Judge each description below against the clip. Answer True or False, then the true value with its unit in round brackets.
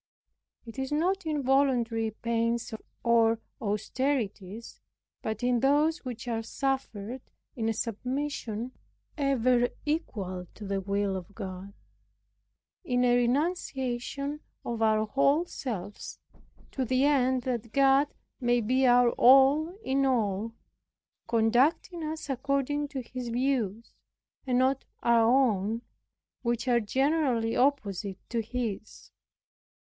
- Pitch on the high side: True (245 Hz)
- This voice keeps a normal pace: False (115 wpm)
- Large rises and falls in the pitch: False (3.4 semitones)